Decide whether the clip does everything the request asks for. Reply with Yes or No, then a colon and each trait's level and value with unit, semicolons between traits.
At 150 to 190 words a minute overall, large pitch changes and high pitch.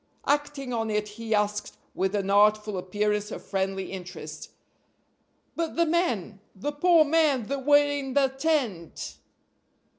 No: average, 140 wpm; wide, 6.0 semitones; high, 225 Hz